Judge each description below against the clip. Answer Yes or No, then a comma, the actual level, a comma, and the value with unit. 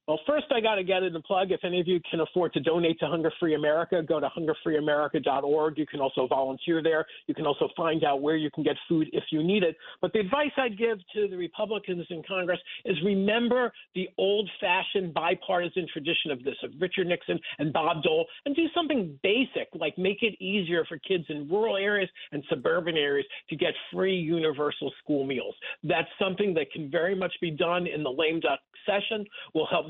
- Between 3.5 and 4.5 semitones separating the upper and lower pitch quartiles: Yes, average, 4.2 semitones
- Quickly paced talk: Yes, fast, 210 wpm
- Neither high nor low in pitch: Yes, medium, 175 Hz